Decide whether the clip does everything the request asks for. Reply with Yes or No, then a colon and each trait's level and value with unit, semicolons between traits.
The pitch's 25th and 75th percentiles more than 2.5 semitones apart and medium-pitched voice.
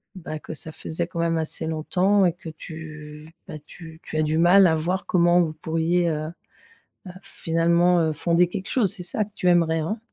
No: narrow, 1.9 semitones; medium, 165 Hz